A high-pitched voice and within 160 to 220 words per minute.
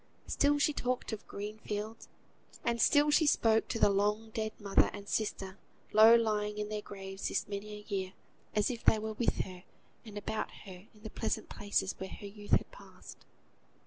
Yes: high, 210 Hz; average, 190 wpm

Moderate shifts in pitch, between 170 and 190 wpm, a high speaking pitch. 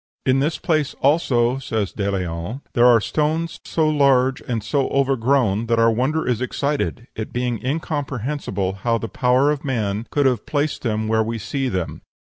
No: average, 4.0 semitones; average, 175 wpm; low, 125 Hz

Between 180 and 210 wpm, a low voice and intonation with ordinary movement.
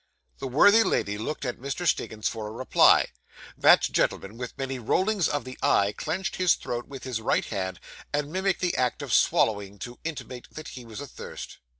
No: average, 190 wpm; low, 130 Hz; wide, 5.8 semitones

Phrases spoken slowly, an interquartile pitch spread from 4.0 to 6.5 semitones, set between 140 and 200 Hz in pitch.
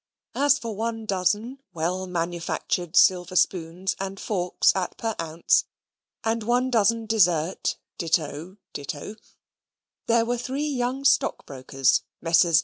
Yes: slow, 120 wpm; average, 5.2 semitones; high, 190 Hz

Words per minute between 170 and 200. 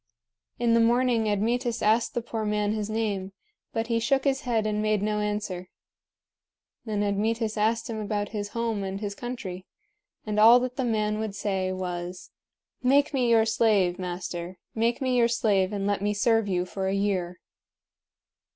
Yes: average, 175 wpm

